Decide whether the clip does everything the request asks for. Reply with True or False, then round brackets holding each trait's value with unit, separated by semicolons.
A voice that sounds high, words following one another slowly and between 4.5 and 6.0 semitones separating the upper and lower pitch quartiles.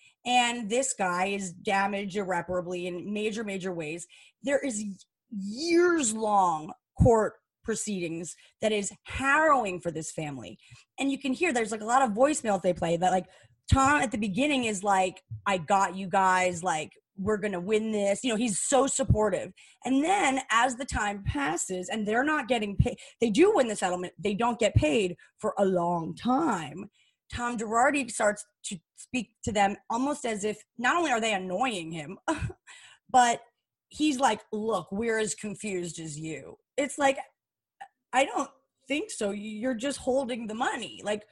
False (215 Hz; 170 wpm; 5.6 semitones)